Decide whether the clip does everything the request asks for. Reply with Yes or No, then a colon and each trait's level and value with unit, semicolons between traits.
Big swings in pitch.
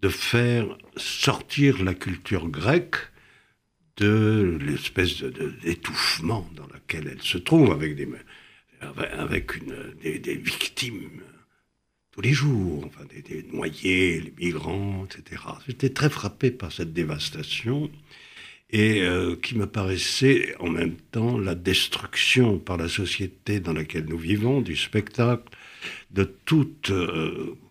Yes: wide, 5.8 semitones